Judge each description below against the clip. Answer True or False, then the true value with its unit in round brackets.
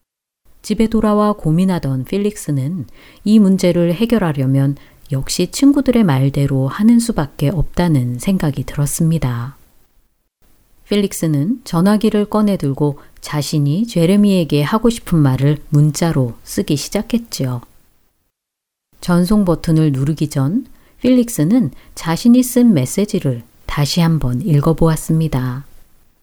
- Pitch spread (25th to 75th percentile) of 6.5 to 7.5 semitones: True (6.8 semitones)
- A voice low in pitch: False (160 Hz)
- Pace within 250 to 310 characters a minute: True (260 characters per minute)